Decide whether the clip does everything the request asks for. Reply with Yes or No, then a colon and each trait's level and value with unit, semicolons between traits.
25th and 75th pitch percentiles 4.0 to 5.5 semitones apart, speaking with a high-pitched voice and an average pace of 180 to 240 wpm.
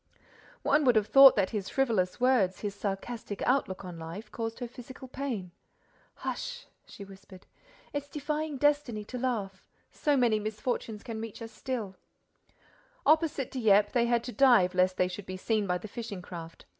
No: average, 4.8 semitones; high, 225 Hz; average, 165 wpm